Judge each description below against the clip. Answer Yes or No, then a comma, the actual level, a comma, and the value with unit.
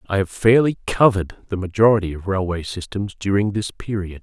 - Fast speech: No, average, 170 wpm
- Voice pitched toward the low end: Yes, low, 100 Hz